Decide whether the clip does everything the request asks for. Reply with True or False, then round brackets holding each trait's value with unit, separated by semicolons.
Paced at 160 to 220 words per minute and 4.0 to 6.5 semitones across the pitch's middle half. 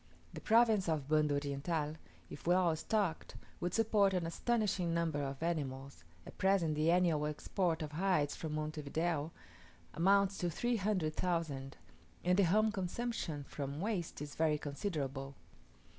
False (145 wpm; 4.3 semitones)